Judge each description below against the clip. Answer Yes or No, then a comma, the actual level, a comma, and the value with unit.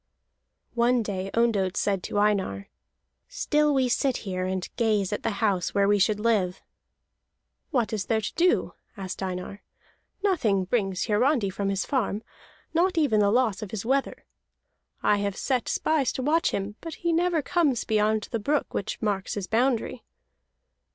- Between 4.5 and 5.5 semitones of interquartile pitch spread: Yes, average, 4.9 semitones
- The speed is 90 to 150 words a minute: No, average, 165 wpm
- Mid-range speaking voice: No, high, 215 Hz